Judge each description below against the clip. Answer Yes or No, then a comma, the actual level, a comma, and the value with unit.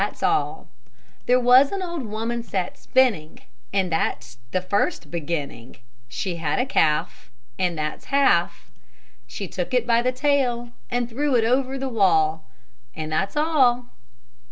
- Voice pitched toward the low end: No, high, 230 Hz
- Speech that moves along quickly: No, average, 150 wpm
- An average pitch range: No, wide, 7.7 semitones